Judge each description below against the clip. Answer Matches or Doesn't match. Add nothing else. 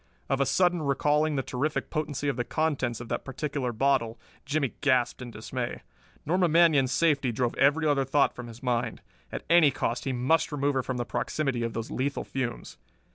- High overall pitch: Doesn't match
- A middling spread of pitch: Matches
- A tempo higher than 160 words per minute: Matches